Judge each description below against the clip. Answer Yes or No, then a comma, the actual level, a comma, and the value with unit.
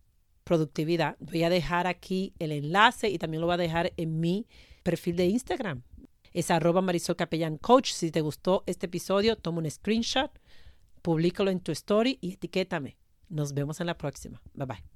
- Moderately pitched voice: Yes, medium, 175 Hz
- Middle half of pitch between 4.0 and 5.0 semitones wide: No, narrow, 2.5 semitones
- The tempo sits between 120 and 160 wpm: No, average, 175 wpm